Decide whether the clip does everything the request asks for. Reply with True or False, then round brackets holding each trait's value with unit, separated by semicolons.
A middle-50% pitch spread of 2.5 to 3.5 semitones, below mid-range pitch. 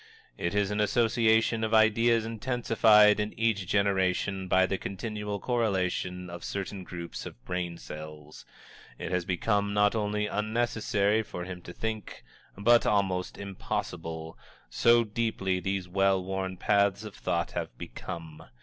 True (3.2 semitones; 100 Hz)